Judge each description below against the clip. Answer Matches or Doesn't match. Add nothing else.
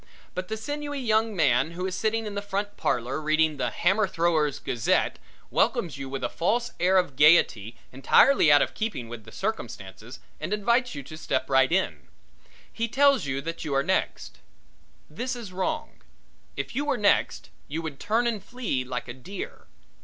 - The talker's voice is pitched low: Doesn't match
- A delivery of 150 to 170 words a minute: Doesn't match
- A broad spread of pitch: Matches